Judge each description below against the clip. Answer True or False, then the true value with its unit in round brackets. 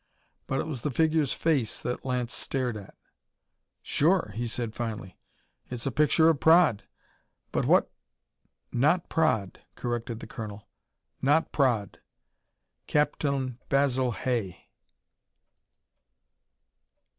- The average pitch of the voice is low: True (130 Hz)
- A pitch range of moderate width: True (4.4 semitones)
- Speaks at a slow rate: True (110 wpm)